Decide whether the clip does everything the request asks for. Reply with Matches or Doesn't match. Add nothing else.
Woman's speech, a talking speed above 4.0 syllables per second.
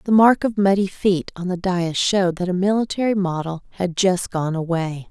Matches